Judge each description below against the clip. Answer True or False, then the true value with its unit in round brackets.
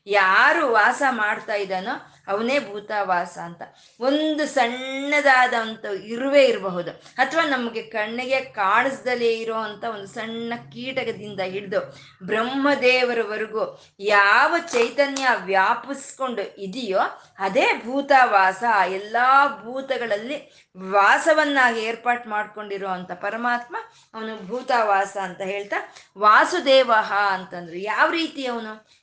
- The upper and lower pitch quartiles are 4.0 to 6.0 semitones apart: True (4.6 semitones)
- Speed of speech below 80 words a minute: False (90 wpm)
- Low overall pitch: False (230 Hz)